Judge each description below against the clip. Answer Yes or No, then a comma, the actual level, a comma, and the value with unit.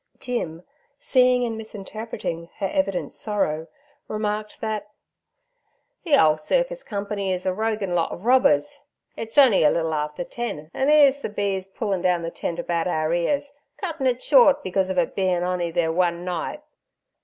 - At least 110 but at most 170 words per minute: Yes, average, 165 wpm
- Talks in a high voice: Yes, high, 195 Hz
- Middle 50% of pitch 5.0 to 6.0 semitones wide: Yes, wide, 5.6 semitones